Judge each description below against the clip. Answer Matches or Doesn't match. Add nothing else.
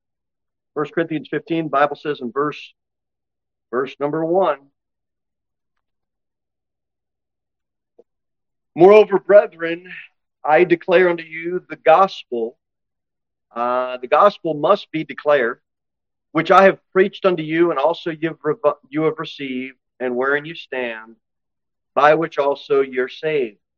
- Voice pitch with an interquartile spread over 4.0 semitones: Matches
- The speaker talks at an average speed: Doesn't match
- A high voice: Doesn't match